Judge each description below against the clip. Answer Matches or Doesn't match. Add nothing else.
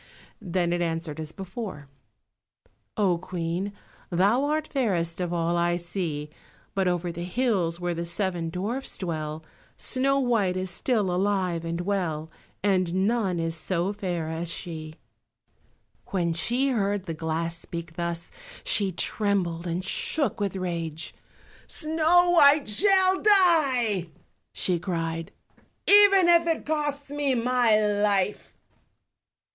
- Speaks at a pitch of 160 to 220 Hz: Matches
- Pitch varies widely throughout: Matches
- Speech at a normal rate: Doesn't match